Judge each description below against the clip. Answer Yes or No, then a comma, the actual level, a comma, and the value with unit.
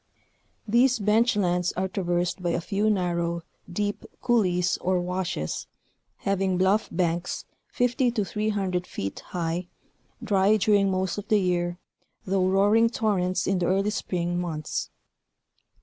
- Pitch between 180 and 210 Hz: Yes, high, 190 Hz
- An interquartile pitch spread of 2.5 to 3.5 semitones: Yes, average, 2.8 semitones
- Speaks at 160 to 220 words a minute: No, average, 140 wpm